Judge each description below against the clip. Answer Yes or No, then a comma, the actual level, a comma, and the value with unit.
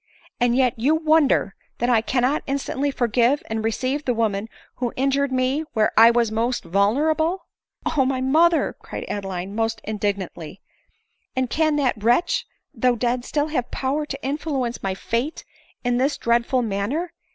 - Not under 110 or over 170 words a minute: Yes, average, 165 wpm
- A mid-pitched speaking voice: No, very high, 250 Hz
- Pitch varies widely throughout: No, average, 3.9 semitones